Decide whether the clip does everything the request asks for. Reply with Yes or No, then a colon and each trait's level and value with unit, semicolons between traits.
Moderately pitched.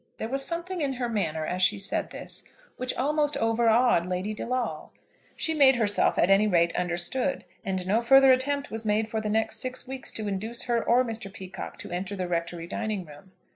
No: high, 220 Hz